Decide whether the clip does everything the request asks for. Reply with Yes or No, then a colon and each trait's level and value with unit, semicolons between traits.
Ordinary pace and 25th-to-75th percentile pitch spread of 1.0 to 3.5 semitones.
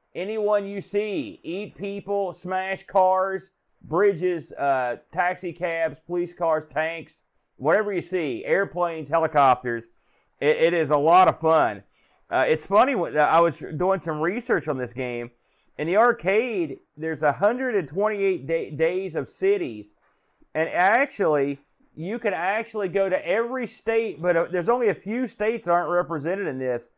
No: average, 150 wpm; average, 4.4 semitones